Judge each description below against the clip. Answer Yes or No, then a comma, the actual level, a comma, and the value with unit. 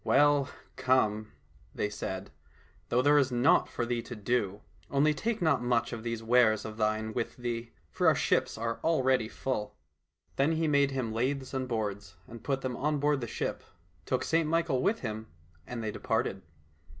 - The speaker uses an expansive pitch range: No, average, 4.2 semitones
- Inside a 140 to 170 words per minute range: No, average, 185 wpm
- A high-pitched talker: No, low, 125 Hz